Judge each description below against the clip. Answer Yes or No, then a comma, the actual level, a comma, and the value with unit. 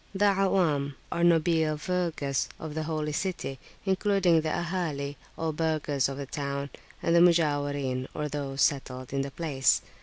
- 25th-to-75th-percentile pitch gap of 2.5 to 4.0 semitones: Yes, average, 3.5 semitones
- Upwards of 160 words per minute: No, average, 155 wpm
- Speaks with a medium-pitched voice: Yes, medium, 155 Hz